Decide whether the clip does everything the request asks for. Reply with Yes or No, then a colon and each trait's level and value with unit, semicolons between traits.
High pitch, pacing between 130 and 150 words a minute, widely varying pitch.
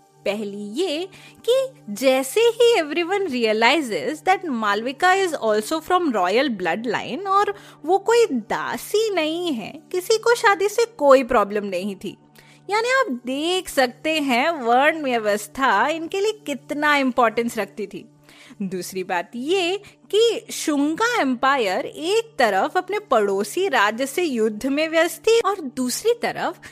Yes: very high, 295 Hz; average, 135 wpm; wide, 8.2 semitones